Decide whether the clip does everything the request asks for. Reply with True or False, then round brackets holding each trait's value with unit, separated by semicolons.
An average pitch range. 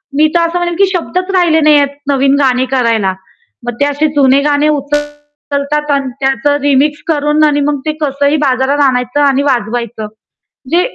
False (2.0 semitones)